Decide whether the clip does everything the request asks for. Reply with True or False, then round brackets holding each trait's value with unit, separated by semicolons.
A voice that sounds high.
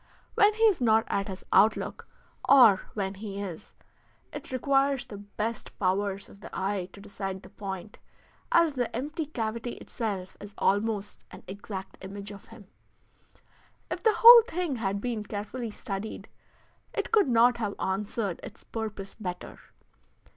True (210 Hz)